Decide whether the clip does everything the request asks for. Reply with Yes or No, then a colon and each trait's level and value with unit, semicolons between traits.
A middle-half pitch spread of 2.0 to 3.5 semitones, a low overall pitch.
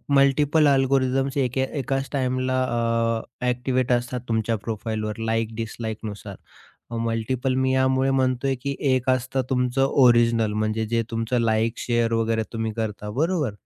Yes: average, 2.7 semitones; low, 120 Hz